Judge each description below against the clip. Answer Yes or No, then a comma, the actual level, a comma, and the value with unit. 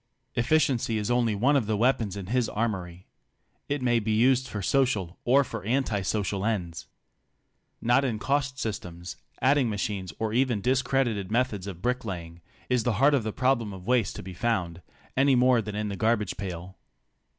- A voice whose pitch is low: Yes, low, 110 Hz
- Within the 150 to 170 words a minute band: No, average, 180 wpm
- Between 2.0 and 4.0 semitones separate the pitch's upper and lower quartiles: No, average, 4.4 semitones